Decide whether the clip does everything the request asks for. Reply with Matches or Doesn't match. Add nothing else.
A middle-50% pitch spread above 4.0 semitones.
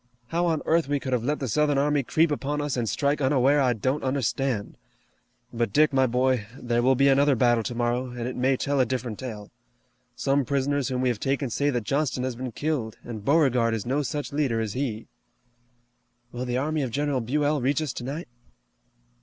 Doesn't match